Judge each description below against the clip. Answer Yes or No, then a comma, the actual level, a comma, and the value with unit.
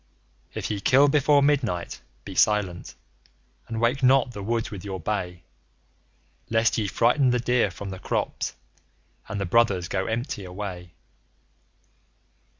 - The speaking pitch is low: Yes, low, 105 Hz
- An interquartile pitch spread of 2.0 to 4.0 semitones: No, average, 4.4 semitones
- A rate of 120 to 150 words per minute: Yes, average, 140 wpm